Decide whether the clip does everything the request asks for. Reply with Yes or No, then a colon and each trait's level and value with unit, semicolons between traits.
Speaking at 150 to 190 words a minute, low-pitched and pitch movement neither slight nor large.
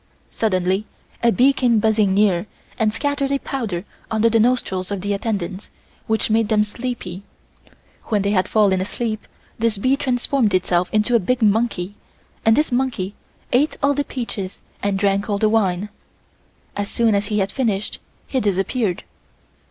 No: average, 160 wpm; high, 215 Hz; average, 3.4 semitones